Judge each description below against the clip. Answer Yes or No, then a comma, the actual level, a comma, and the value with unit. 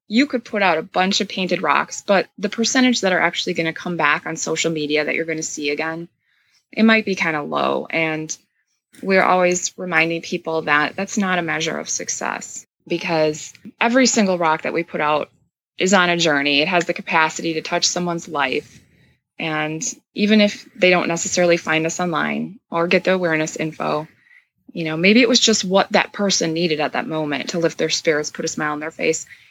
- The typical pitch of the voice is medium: Yes, medium, 170 Hz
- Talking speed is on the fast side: Yes, fast, 210 wpm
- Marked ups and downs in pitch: No, average, 3.8 semitones